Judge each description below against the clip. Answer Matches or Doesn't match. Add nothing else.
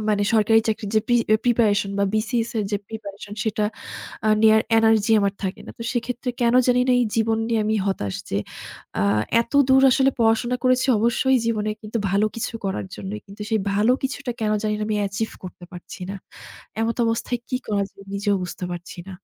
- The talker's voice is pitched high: Matches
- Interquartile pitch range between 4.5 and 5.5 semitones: Doesn't match